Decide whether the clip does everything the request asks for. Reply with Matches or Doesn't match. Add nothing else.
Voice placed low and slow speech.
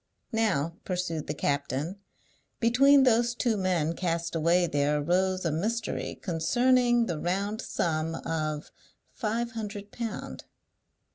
Doesn't match